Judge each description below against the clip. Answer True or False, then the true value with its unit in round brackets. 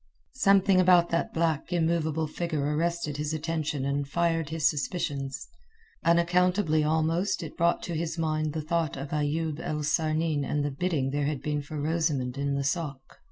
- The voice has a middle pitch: True (155 Hz)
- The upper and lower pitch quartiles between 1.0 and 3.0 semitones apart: True (2.5 semitones)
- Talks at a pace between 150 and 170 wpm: True (165 wpm)